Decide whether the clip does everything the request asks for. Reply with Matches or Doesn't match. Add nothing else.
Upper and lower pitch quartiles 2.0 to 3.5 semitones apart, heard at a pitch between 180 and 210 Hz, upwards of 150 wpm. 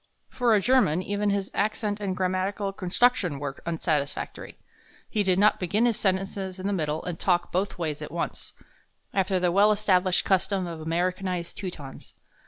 Matches